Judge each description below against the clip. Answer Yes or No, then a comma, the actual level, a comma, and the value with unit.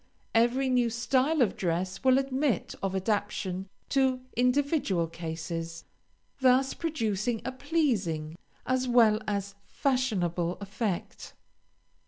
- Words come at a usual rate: No, slow, 105 wpm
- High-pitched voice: Yes, high, 230 Hz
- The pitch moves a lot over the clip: Yes, wide, 5.8 semitones